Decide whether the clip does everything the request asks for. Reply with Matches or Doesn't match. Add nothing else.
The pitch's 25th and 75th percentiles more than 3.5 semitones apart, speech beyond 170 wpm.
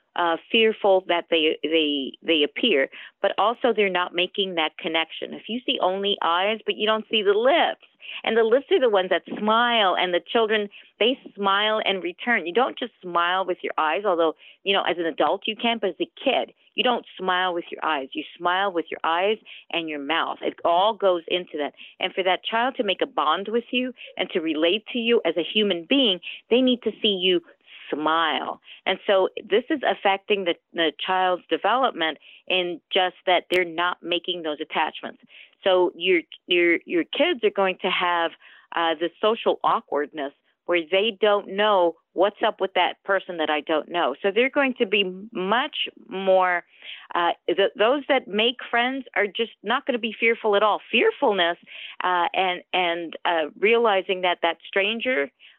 Matches